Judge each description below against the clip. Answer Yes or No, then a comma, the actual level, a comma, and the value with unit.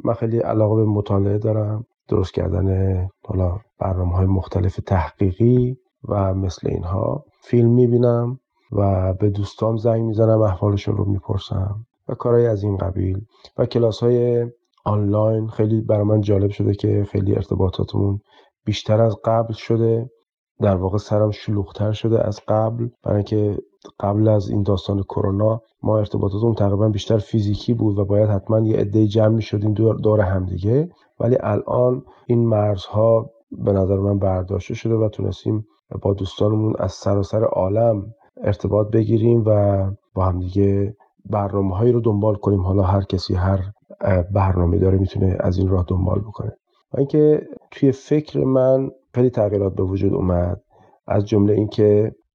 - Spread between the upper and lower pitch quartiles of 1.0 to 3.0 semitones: Yes, narrow, 2.4 semitones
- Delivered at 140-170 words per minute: Yes, average, 150 wpm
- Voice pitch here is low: Yes, low, 105 Hz